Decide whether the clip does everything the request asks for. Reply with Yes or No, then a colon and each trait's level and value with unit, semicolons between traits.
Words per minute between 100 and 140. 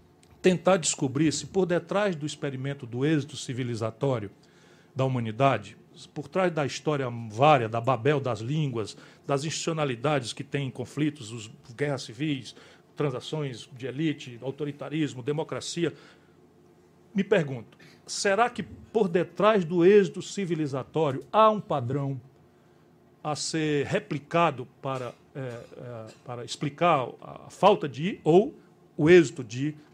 Yes: slow, 120 wpm